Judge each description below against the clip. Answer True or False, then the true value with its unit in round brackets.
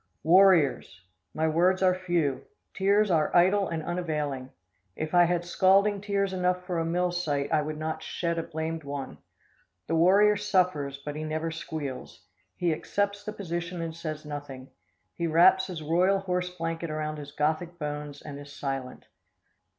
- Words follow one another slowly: False (165 wpm)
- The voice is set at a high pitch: False (165 Hz)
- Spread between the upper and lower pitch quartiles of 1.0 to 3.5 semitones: True (3.2 semitones)